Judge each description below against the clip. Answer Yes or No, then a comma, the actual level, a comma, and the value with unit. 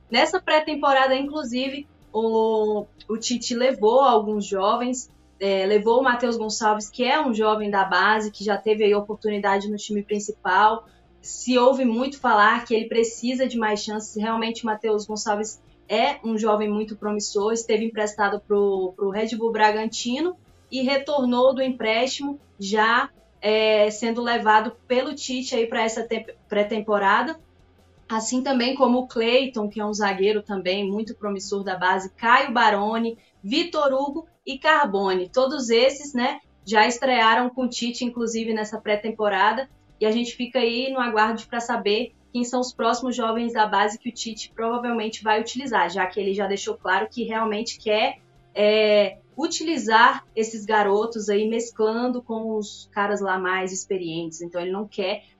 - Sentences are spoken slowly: No, average, 160 wpm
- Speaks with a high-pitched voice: Yes, high, 220 Hz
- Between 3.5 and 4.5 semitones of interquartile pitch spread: No, average, 2.8 semitones